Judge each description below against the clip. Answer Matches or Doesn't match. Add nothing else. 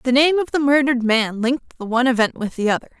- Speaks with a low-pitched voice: Doesn't match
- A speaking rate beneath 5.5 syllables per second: Doesn't match